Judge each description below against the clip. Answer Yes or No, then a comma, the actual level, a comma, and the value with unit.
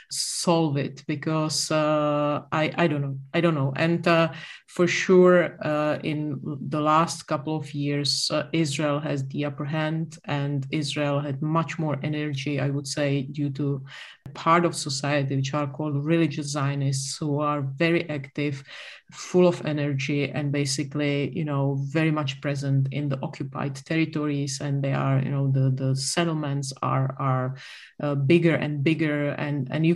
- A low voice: No, medium, 145 Hz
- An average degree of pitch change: No, narrow, 1.9 semitones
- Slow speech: No, average, 165 wpm